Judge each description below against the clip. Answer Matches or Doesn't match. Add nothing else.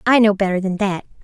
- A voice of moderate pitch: Doesn't match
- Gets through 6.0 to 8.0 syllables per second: Matches